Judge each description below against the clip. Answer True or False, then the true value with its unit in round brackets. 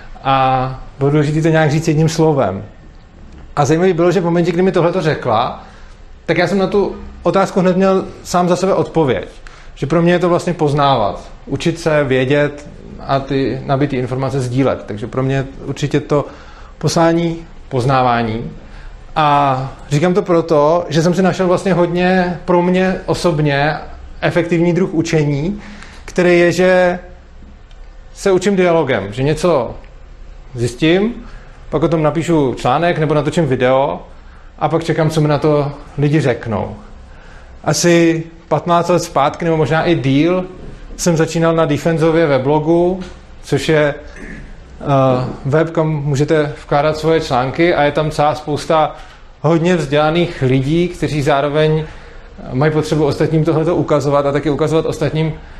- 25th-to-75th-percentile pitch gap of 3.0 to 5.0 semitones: True (3.7 semitones)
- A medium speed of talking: True (150 wpm)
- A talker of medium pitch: True (155 Hz)